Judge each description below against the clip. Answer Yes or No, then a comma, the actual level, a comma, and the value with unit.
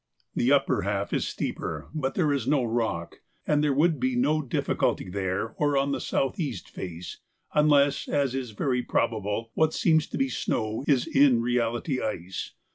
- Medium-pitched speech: No, low, 130 Hz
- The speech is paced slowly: No, average, 175 wpm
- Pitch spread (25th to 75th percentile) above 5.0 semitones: No, average, 4.4 semitones